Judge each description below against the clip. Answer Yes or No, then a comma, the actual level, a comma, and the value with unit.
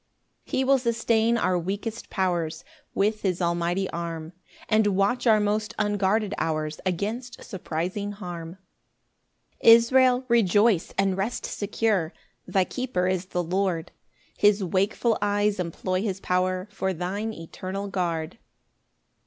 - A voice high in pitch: Yes, high, 195 Hz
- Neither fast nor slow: No, slow, 130 wpm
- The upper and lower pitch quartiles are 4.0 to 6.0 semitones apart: No, average, 3.4 semitones